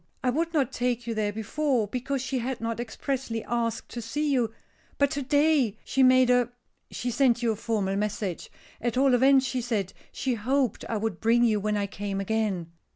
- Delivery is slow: No, average, 200 wpm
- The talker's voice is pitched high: Yes, high, 240 Hz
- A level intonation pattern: No, average, 3.4 semitones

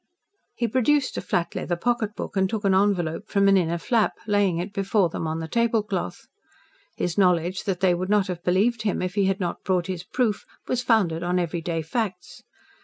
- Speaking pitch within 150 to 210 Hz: Yes, high, 190 Hz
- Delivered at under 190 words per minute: No, average, 195 wpm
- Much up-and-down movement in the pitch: No, average, 3.3 semitones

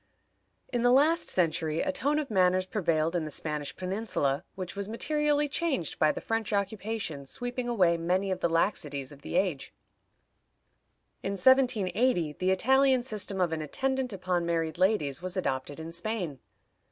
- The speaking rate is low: No, average, 160 wpm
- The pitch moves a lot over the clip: Yes, wide, 6.5 semitones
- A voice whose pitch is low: No, medium, 185 Hz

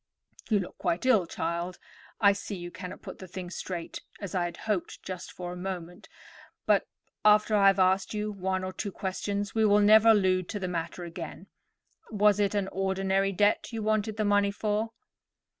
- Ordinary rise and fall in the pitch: No, narrow, 2.3 semitones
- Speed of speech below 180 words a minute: No, average, 190 wpm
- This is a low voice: No, high, 195 Hz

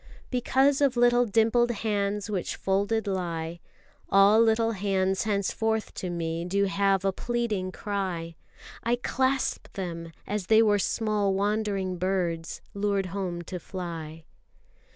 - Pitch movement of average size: Yes, average, 3.2 semitones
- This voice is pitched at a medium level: No, high, 200 Hz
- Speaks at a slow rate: Yes, slow, 130 wpm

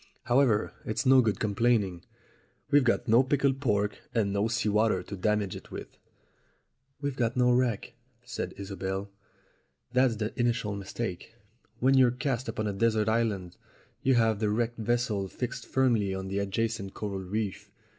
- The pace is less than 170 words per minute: Yes, average, 155 wpm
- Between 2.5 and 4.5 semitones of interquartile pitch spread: Yes, average, 3.3 semitones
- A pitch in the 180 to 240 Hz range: No, low, 110 Hz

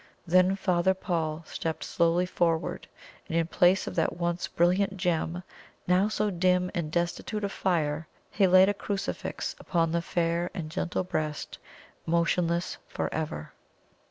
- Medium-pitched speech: Yes, medium, 175 Hz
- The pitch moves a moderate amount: No, narrow, 1.8 semitones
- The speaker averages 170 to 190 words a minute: No, average, 145 wpm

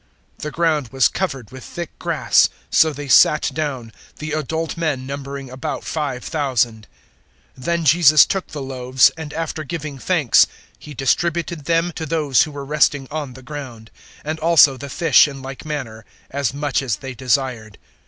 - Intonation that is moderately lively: Yes, average, 3.1 semitones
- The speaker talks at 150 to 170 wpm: Yes, average, 165 wpm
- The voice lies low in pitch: No, medium, 145 Hz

